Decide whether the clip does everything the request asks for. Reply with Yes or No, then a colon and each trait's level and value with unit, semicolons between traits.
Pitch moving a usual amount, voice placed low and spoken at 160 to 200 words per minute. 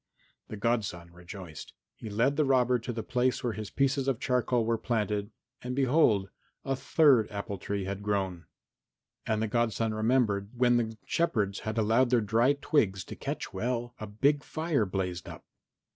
Yes: average, 3.7 semitones; low, 115 Hz; average, 175 wpm